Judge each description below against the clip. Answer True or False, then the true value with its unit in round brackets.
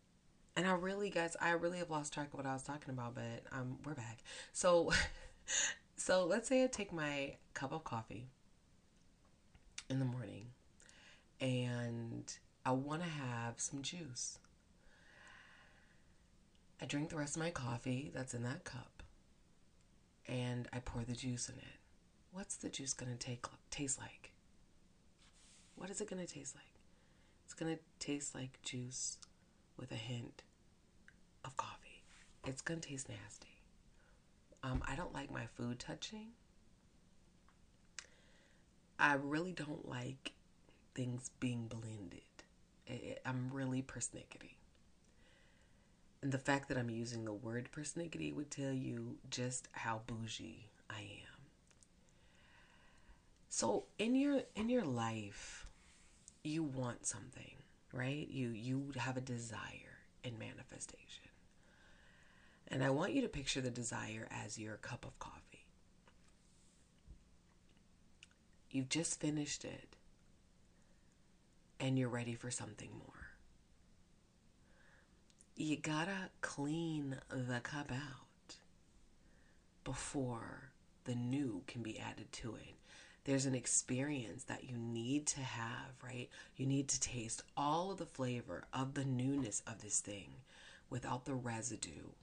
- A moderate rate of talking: False (130 wpm)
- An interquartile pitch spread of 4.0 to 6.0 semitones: False (3.6 semitones)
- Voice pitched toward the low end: True (130 Hz)